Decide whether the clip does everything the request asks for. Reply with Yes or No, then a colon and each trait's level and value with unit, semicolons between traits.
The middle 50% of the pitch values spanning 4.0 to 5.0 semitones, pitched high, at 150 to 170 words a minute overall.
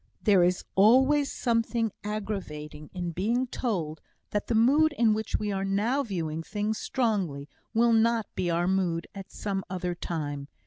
Yes: average, 4.7 semitones; high, 205 Hz; average, 160 wpm